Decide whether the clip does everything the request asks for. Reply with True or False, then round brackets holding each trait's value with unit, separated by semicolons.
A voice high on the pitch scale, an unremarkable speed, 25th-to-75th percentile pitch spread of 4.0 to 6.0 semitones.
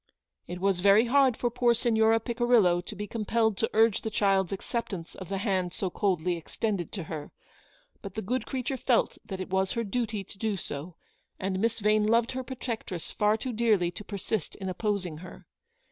False (210 Hz; 195 wpm; 3.6 semitones)